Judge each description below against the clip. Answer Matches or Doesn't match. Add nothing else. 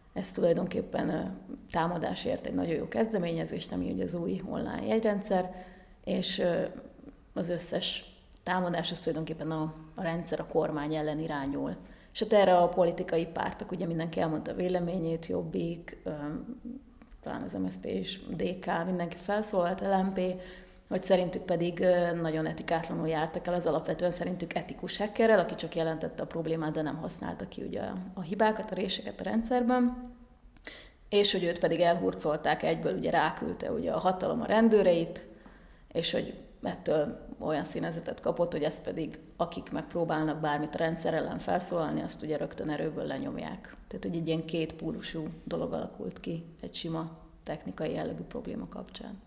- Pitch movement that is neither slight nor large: Matches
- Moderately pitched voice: Matches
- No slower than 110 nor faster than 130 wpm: Doesn't match